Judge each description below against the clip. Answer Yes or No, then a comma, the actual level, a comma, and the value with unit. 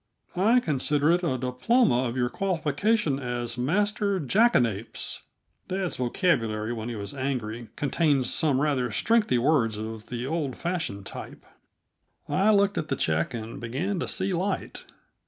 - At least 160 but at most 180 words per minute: No, average, 145 wpm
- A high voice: No, medium, 140 Hz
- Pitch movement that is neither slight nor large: No, wide, 7.3 semitones